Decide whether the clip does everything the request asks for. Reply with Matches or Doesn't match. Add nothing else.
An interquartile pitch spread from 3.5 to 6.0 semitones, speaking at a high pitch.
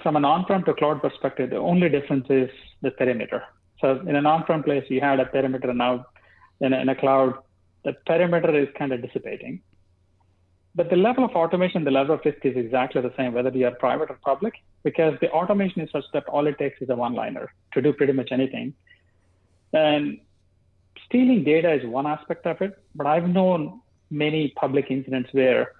Doesn't match